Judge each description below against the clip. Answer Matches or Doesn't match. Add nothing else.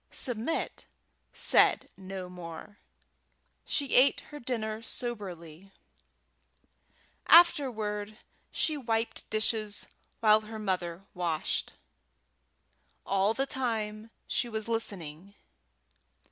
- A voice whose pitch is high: Matches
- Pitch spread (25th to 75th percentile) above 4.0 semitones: Doesn't match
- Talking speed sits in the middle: Doesn't match